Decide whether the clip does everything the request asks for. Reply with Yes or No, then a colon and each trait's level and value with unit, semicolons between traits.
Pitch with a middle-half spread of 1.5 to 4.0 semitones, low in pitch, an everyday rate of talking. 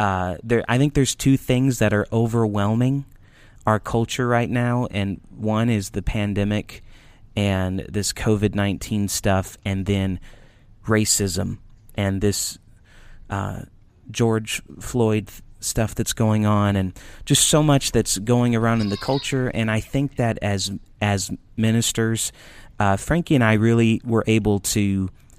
Yes: average, 2.7 semitones; low, 110 Hz; average, 145 wpm